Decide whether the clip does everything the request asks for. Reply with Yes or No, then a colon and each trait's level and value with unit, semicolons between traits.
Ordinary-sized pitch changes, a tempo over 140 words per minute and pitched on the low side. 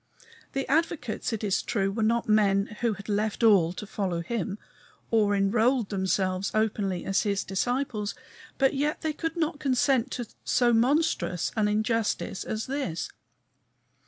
No: average, 4.3 semitones; average, 150 wpm; high, 220 Hz